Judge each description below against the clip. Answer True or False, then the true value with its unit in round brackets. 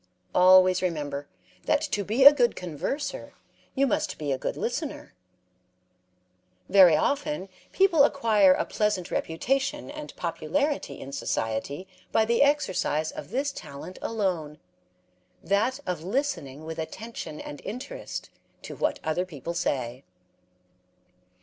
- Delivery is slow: True (125 wpm)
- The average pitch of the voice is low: False (190 Hz)